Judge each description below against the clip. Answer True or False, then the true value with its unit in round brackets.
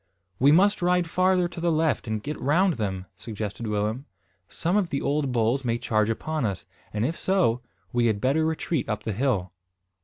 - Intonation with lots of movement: True (7.0 semitones)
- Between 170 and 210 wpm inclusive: True (190 wpm)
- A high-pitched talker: False (135 Hz)